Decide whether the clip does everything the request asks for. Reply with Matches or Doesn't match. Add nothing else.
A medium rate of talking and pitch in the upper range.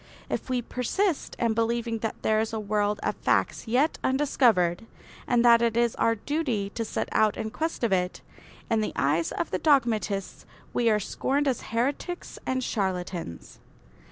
Matches